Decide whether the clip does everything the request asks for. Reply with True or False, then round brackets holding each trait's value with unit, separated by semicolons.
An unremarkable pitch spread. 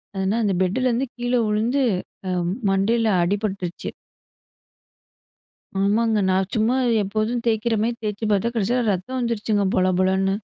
True (3.2 semitones)